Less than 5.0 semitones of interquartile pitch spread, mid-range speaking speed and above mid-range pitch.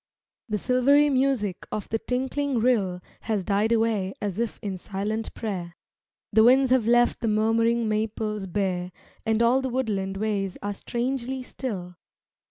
Yes: average, 3.8 semitones; average, 150 wpm; high, 220 Hz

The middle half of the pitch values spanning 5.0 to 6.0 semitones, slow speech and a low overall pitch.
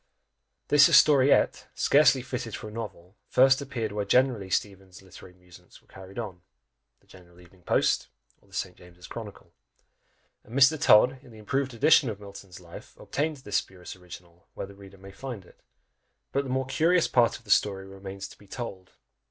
No: wide, 5.6 semitones; average, 185 wpm; low, 105 Hz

